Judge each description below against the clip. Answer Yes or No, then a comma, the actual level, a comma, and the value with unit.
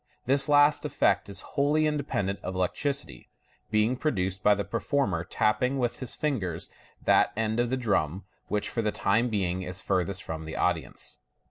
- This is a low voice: Yes, low, 105 Hz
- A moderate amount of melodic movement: No, wide, 5.9 semitones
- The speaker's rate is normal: Yes, average, 165 wpm